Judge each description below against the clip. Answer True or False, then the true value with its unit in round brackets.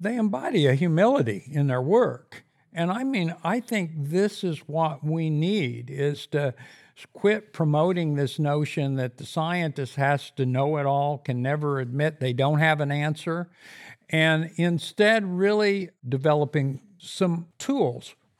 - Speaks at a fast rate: False (145 wpm)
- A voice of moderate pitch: True (155 Hz)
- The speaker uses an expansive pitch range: False (4.0 semitones)